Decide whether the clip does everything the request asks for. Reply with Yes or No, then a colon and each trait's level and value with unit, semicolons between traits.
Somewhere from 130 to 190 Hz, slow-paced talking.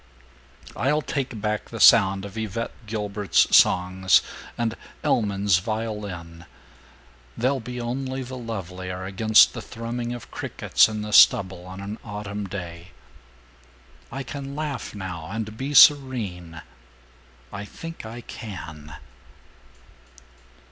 No: low, 105 Hz; slow, 115 wpm